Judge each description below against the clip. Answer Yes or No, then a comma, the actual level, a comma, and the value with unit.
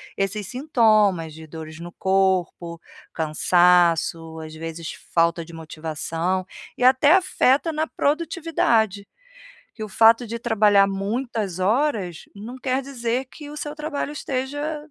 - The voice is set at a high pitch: Yes, high, 210 Hz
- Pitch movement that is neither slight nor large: No, wide, 7.6 semitones